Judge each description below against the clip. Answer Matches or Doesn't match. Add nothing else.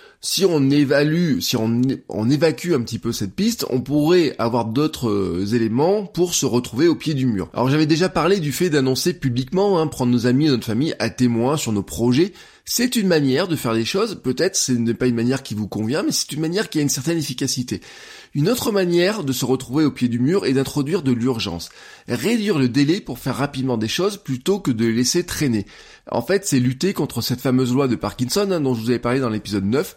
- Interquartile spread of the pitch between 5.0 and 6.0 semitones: Matches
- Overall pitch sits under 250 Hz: Matches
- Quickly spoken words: Matches